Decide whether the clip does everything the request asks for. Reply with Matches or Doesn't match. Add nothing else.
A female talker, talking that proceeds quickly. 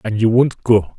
Doesn't match